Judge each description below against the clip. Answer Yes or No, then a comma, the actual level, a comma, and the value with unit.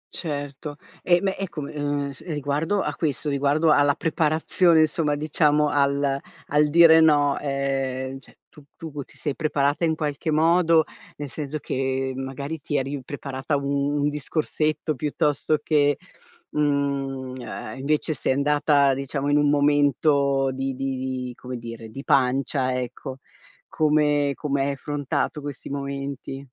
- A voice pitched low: No, medium, 145 Hz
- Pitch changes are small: Yes, narrow, 1.8 semitones